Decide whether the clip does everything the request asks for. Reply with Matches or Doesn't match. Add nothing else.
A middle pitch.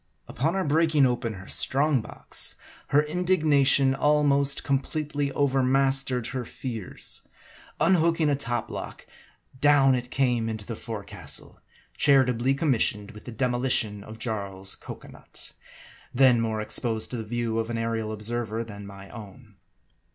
Doesn't match